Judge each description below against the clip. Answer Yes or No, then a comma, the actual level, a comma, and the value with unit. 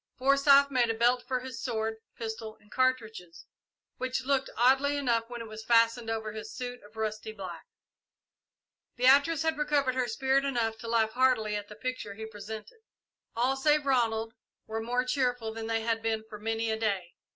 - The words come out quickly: No, average, 180 wpm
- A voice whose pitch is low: No, high, 230 Hz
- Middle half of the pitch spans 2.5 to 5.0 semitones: Yes, average, 2.8 semitones